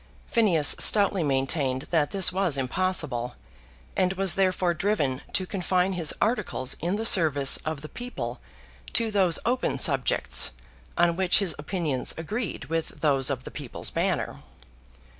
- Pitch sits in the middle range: Yes, medium, 175 Hz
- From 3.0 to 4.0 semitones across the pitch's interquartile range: No, average, 4.9 semitones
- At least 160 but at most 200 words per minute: No, average, 140 wpm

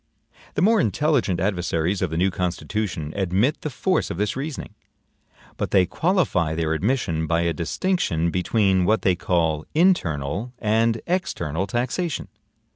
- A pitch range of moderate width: No, wide, 7.1 semitones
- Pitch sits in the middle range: No, very low, 95 Hz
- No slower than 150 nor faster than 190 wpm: No, average, 140 wpm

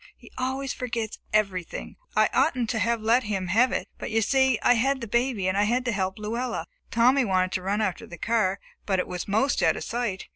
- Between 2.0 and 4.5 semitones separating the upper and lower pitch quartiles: Yes, average, 4.2 semitones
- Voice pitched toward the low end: No, high, 225 Hz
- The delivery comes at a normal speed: No, fast, 220 wpm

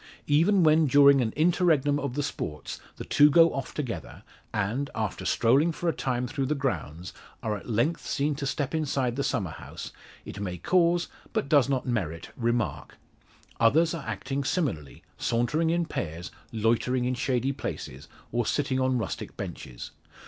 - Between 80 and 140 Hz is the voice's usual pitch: Yes, low, 135 Hz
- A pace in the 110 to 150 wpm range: No, average, 165 wpm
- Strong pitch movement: No, average, 4.7 semitones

